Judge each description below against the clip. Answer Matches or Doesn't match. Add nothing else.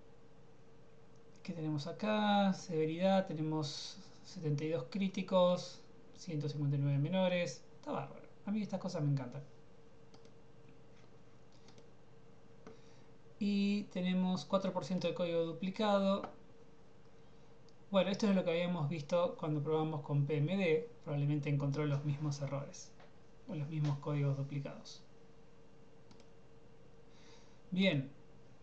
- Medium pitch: Matches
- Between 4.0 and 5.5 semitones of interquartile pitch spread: Doesn't match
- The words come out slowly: Matches